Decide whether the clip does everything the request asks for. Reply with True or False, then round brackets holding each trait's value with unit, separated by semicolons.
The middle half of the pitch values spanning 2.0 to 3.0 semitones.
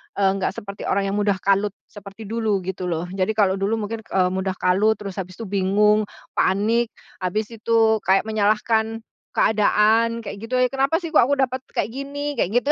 True (2.6 semitones)